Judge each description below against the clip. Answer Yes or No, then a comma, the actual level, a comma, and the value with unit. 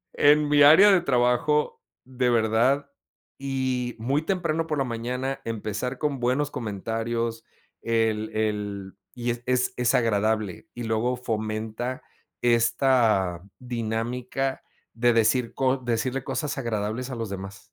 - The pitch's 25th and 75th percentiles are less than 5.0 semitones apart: Yes, average, 3.1 semitones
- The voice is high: No, low, 120 Hz